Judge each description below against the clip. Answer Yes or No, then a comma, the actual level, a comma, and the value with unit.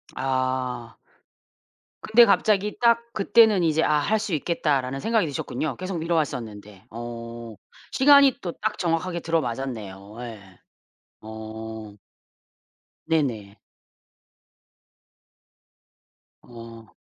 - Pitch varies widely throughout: Yes, wide, 8.1 semitones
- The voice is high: No, low, 135 Hz